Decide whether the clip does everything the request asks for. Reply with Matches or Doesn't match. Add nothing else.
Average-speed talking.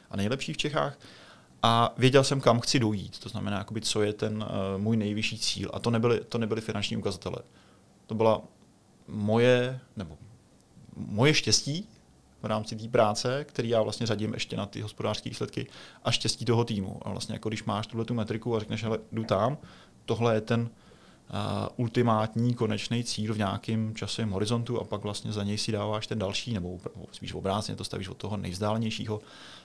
Doesn't match